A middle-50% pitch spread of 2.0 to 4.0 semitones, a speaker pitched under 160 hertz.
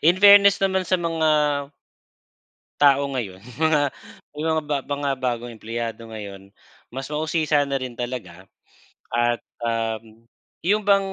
No: wide, 5.5 semitones; low, 135 Hz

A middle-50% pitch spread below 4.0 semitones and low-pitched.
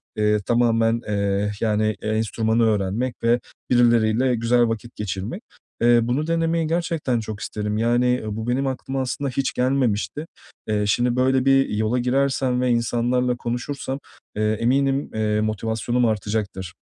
Yes: average, 2.9 semitones; low, 120 Hz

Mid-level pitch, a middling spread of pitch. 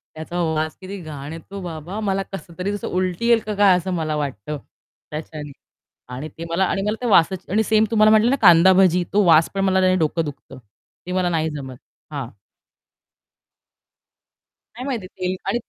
Yes: medium, 180 Hz; average, 3.9 semitones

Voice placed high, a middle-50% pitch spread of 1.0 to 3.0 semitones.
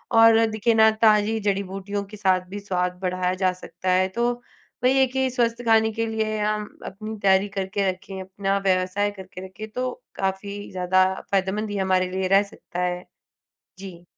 Yes: high, 195 Hz; narrow, 2.6 semitones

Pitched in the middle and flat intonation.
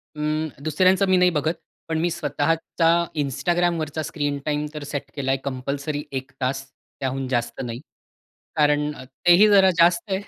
No: medium, 150 Hz; average, 3.7 semitones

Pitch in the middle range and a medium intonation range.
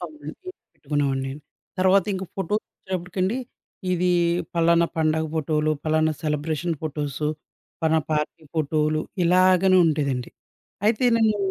Yes: medium, 160 Hz; average, 3.3 semitones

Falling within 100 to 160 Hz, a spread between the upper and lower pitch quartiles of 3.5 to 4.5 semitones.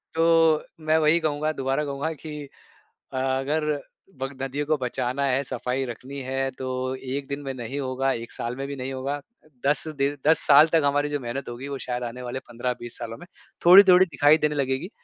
No: low, 135 Hz; narrow, 2.5 semitones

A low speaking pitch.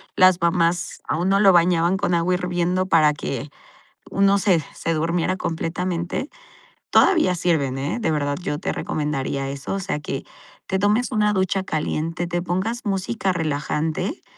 No: medium, 175 Hz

